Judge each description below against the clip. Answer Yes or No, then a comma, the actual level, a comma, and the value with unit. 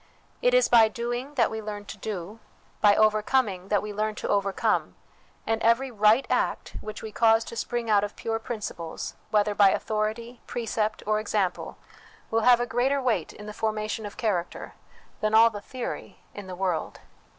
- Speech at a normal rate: Yes, average, 185 wpm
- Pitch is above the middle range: Yes, high, 215 Hz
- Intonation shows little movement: Yes, narrow, 2.0 semitones